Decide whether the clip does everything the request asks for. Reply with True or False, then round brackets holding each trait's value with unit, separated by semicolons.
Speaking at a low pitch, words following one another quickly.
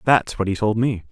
True (105 Hz; 270 wpm)